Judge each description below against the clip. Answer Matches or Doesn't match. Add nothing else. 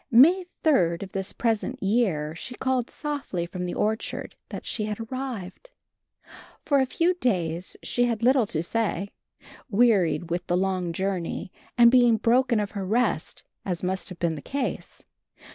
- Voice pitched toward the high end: Matches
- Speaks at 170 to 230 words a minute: Doesn't match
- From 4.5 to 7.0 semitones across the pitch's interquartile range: Matches